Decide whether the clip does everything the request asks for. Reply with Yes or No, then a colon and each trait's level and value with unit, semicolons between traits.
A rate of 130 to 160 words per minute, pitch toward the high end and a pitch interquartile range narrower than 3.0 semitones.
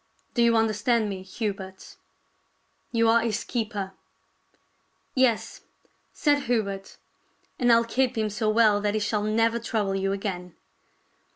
Yes: average, 145 wpm; high, 215 Hz; narrow, 2.6 semitones